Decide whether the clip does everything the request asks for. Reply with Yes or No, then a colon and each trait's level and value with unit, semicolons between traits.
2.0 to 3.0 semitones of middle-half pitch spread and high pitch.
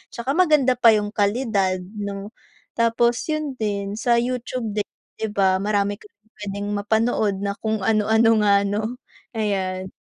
Yes: average, 2.7 semitones; high, 215 Hz